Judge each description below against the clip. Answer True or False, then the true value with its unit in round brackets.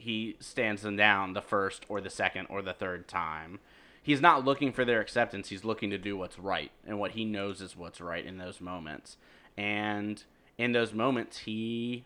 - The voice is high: False (105 Hz)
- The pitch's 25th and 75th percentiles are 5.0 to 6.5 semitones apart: False (3.4 semitones)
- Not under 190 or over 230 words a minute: True (200 wpm)